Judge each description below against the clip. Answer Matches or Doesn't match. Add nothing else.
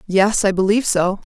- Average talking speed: Matches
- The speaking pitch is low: Doesn't match